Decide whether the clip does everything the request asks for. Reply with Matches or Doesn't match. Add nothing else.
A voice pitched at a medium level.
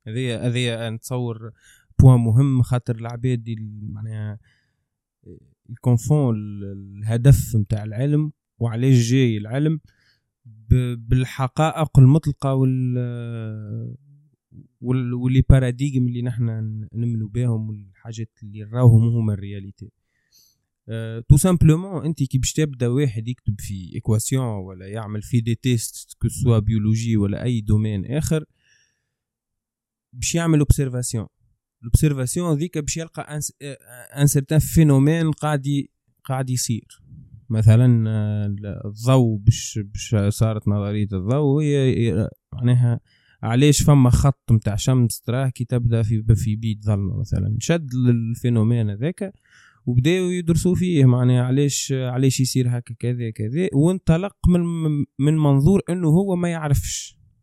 Doesn't match